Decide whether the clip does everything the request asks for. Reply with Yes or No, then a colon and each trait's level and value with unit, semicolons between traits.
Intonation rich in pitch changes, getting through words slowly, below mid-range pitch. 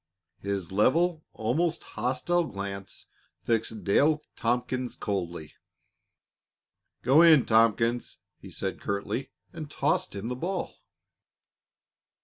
Yes: wide, 7.3 semitones; slow, 100 wpm; low, 120 Hz